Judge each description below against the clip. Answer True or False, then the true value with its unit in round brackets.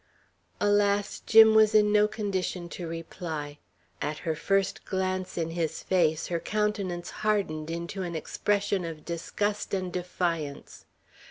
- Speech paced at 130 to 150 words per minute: True (135 wpm)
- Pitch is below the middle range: False (185 Hz)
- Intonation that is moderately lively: True (3.7 semitones)